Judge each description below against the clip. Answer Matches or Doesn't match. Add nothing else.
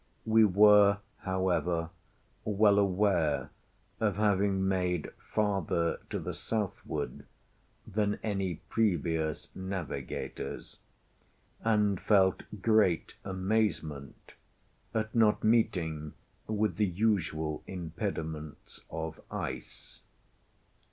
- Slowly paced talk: Matches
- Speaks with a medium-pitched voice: Doesn't match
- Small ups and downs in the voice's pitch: Doesn't match